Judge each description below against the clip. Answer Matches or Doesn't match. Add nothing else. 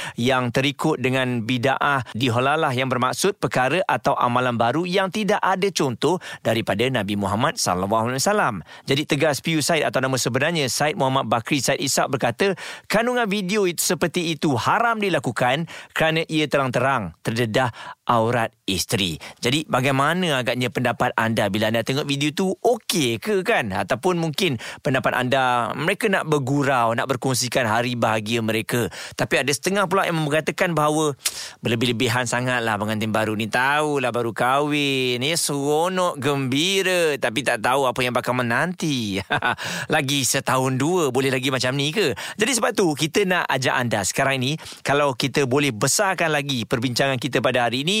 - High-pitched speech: Doesn't match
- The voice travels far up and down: Doesn't match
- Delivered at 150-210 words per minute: Matches